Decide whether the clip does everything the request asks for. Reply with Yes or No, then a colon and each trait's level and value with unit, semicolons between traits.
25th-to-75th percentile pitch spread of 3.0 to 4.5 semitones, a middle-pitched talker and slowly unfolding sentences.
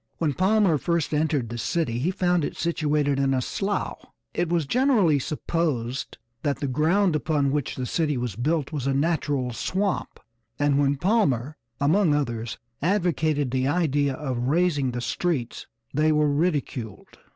No: average, 4.0 semitones; medium, 150 Hz; average, 155 wpm